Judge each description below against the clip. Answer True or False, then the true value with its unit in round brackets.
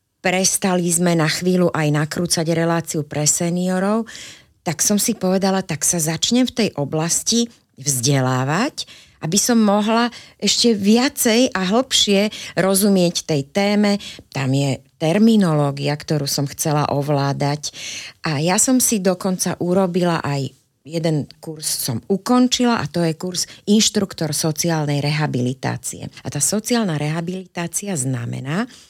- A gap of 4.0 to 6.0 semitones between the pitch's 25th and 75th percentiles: True (5.5 semitones)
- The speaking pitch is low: False (170 Hz)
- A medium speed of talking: True (125 wpm)